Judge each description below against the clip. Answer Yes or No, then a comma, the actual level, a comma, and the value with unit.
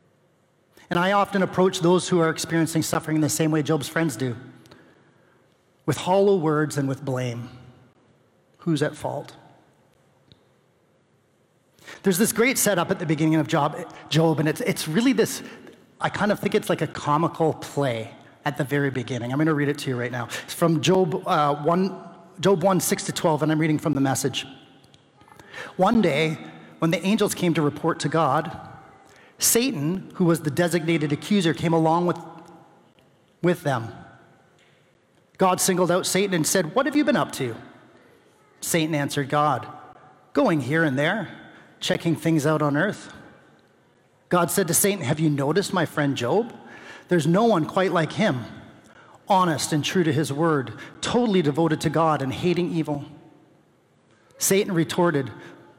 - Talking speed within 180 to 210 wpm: No, average, 165 wpm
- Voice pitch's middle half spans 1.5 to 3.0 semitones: No, average, 3.6 semitones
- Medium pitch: Yes, medium, 165 Hz